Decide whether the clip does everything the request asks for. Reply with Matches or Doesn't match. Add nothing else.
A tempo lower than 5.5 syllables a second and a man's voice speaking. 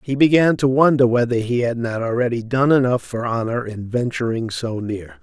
Matches